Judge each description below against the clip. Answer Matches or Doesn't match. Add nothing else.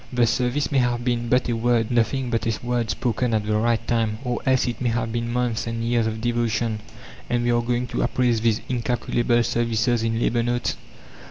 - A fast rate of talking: Matches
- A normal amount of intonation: Doesn't match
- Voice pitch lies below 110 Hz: Doesn't match